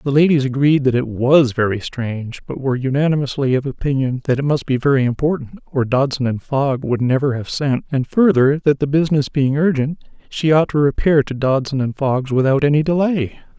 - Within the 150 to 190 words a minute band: No, average, 200 wpm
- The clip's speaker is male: Yes, male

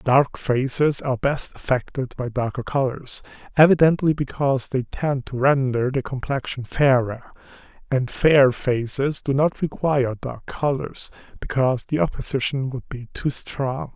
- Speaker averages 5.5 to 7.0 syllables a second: No, 4.5 syllables/s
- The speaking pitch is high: No, low, 135 Hz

